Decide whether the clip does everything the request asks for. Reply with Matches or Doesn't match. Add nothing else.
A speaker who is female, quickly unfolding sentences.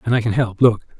Doesn't match